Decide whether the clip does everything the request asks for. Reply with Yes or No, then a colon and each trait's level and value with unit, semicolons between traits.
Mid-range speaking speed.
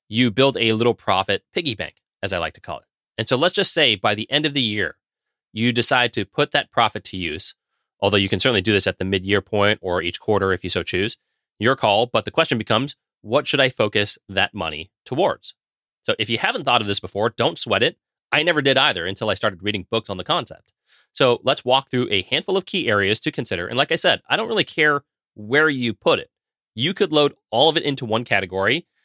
No: fast, 245 wpm